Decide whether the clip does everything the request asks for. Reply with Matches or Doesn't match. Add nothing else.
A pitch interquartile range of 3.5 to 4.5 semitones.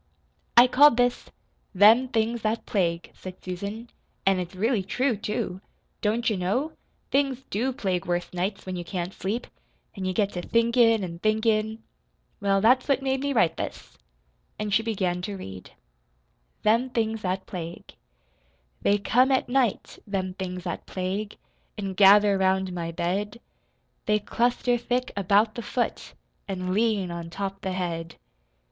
Matches